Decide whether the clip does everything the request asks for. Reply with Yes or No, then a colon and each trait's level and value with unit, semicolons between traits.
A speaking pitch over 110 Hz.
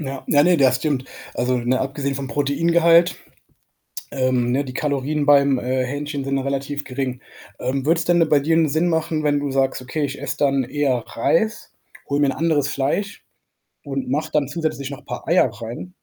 Yes: medium, 140 Hz